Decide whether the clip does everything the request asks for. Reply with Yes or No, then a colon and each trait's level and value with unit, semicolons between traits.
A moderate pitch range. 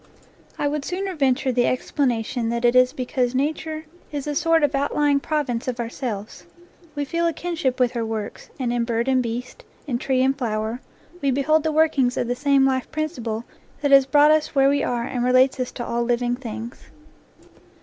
Yes: average, 3.2 semitones